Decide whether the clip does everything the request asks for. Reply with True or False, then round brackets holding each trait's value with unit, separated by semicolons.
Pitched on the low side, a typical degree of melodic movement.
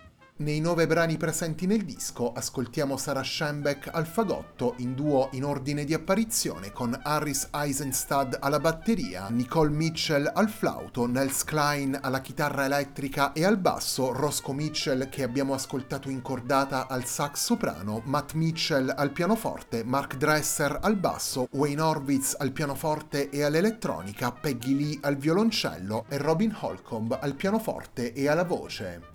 False (145 Hz; 3.1 semitones)